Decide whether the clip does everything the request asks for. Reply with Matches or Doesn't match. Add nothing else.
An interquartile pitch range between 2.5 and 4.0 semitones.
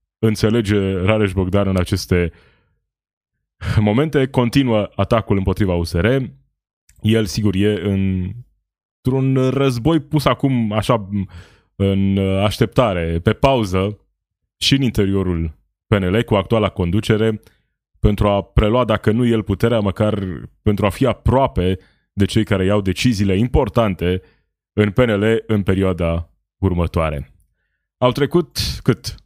Matches